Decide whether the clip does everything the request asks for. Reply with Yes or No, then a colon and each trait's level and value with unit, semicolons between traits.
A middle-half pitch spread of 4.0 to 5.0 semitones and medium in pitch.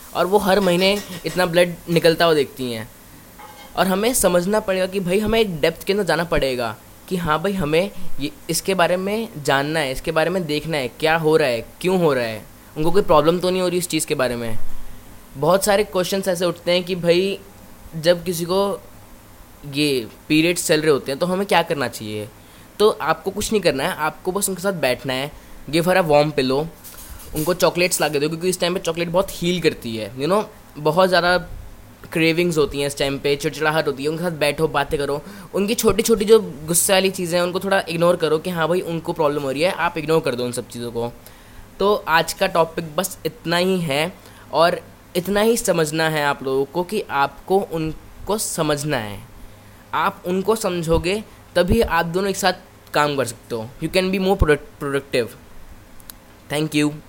Yes: average, 4.5 semitones; medium, 165 Hz